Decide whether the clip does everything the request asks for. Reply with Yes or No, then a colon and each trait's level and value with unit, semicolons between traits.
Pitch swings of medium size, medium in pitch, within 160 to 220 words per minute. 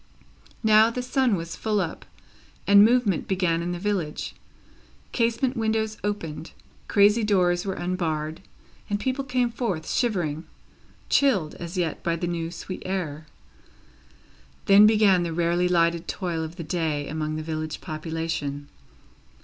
No: average, 4.6 semitones; medium, 180 Hz; average, 140 wpm